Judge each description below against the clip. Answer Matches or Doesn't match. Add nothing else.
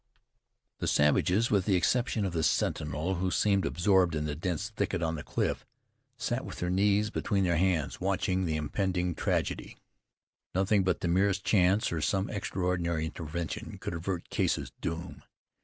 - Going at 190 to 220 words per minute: Doesn't match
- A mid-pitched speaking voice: Doesn't match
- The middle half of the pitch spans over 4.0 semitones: Doesn't match